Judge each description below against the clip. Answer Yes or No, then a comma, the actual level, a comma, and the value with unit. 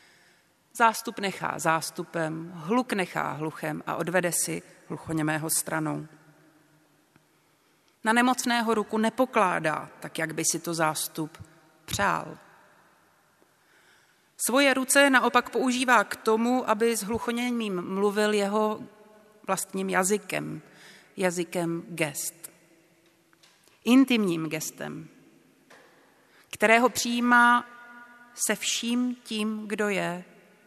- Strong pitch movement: Yes, wide, 5.9 semitones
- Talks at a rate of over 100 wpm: No, slow, 90 wpm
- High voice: Yes, high, 200 Hz